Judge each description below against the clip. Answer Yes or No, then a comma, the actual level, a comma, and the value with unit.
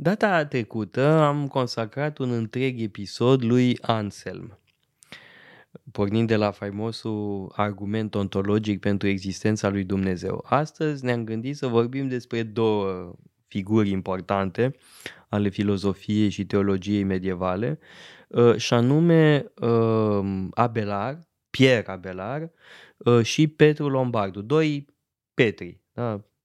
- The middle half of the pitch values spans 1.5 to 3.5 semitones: No, average, 4.5 semitones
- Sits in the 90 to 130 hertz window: Yes, low, 115 Hz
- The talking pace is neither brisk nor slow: No, slow, 100 wpm